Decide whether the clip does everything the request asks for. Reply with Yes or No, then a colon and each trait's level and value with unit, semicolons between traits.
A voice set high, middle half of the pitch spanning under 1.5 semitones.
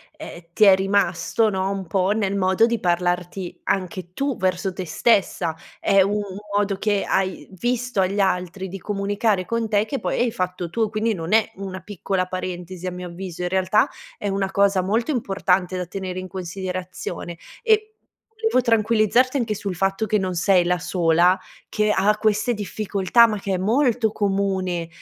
No: high, 195 Hz; average, 2.7 semitones